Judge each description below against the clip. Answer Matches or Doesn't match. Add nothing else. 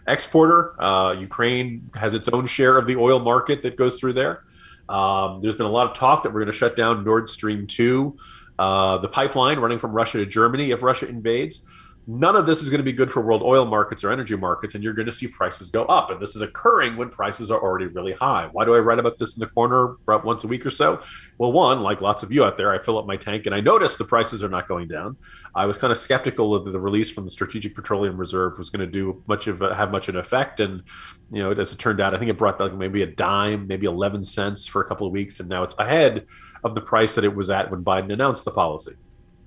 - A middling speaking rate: Doesn't match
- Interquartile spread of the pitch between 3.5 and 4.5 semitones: Matches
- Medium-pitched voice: Doesn't match